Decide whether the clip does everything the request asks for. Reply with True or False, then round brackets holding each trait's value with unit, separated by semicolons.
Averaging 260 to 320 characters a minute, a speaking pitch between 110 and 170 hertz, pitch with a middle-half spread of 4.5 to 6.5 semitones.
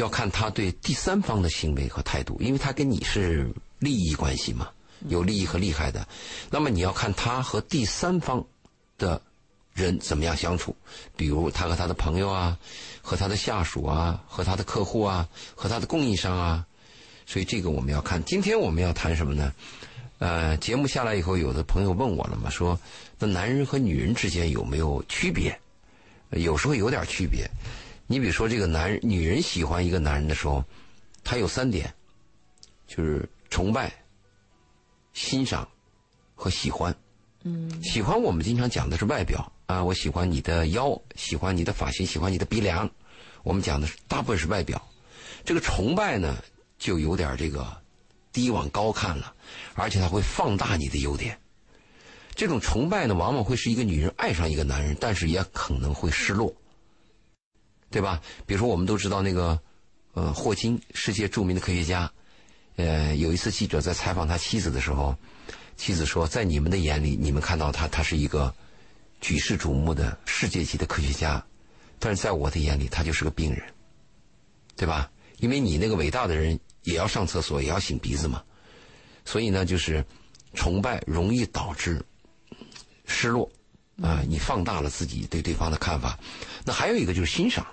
False (270 characters per minute; 90 Hz; 5.2 semitones)